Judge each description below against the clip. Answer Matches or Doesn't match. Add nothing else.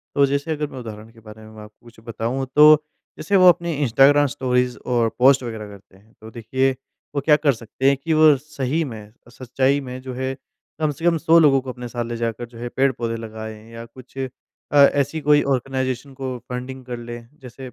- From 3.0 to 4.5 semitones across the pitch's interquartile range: Matches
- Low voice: Matches